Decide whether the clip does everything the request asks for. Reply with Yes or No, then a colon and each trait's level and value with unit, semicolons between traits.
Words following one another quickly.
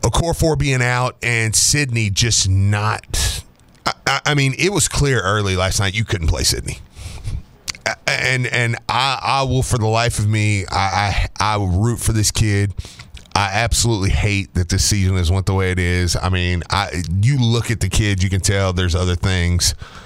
No: average, 195 wpm